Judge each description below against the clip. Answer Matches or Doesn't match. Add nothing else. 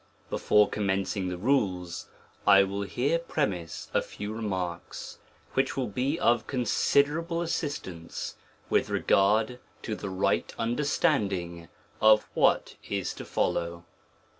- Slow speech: Matches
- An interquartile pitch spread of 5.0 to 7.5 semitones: Matches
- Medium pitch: Doesn't match